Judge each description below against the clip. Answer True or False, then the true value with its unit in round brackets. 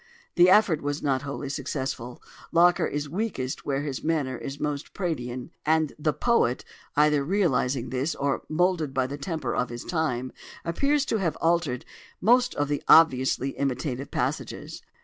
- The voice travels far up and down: False (4.2 semitones)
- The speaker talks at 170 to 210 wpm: False (155 wpm)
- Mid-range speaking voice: True (145 Hz)